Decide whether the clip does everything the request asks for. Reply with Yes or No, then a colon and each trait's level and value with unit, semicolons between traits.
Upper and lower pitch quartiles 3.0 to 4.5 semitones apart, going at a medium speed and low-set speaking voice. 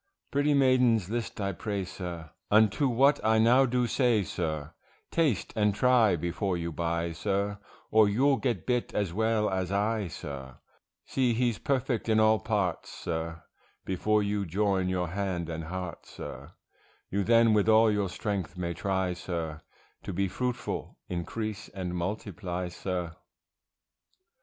Yes: average, 4.2 semitones; average, 145 wpm; low, 100 Hz